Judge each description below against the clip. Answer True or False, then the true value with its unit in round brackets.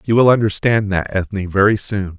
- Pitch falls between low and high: False (100 Hz)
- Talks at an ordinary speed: True (190 wpm)